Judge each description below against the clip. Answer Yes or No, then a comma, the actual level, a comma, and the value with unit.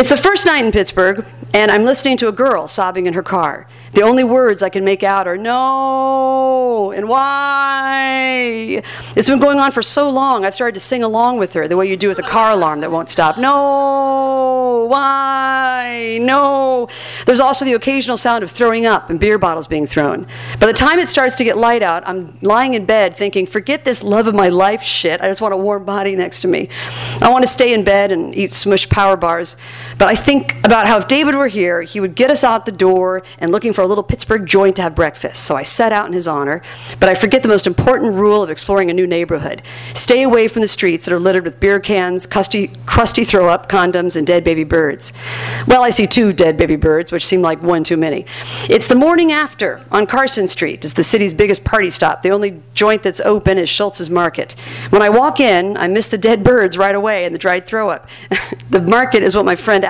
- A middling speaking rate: No, fast, 230 wpm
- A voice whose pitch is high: Yes, high, 205 Hz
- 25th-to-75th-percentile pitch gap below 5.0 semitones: No, wide, 5.4 semitones